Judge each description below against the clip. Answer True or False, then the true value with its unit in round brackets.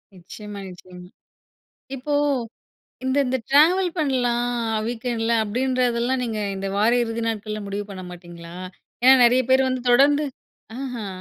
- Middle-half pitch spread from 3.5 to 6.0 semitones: True (4.0 semitones)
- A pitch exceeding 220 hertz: True (235 Hz)